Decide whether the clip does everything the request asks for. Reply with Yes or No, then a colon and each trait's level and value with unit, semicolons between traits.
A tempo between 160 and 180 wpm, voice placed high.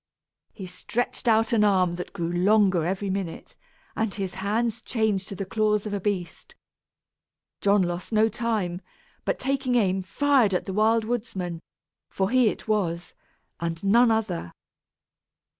No: average, 150 wpm; high, 200 Hz